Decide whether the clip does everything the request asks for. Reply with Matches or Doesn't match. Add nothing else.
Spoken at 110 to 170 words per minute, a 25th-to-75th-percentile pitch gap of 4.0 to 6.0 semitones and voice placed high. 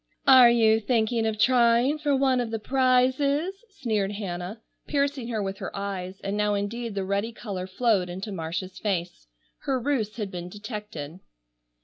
Matches